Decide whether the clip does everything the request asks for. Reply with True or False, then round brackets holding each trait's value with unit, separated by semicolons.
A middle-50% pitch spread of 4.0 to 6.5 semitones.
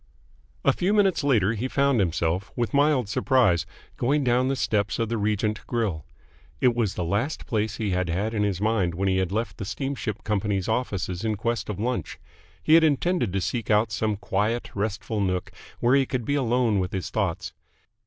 True (4.3 semitones)